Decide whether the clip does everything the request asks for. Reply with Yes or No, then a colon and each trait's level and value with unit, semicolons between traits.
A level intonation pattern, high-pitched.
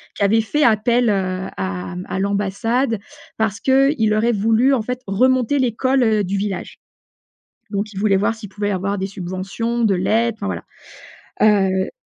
No: average, 3.3 semitones; high, 210 Hz